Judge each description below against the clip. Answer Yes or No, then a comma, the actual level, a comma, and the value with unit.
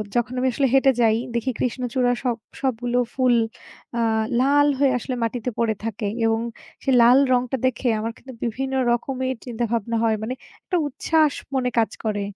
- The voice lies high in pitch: Yes, high, 245 Hz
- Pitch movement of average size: No, narrow, 2.3 semitones